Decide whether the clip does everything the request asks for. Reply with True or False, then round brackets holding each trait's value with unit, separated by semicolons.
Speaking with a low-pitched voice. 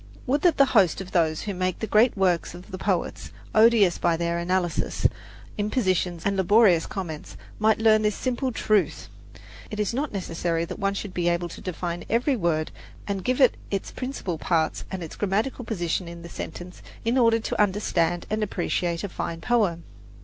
False (190 Hz)